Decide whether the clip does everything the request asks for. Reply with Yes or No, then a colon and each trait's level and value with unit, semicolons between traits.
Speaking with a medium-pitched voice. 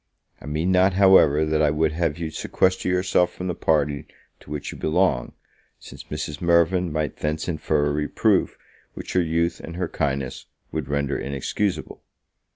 No: very low, 80 Hz